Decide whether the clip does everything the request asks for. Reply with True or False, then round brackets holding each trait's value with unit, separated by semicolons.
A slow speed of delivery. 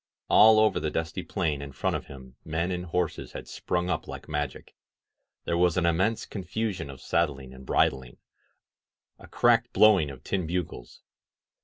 False (175 wpm)